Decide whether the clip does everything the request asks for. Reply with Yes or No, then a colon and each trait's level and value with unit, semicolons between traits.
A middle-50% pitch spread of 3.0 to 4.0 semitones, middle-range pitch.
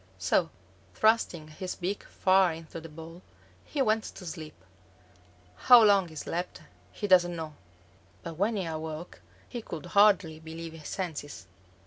Yes: average, 3.6 semitones; medium, 170 Hz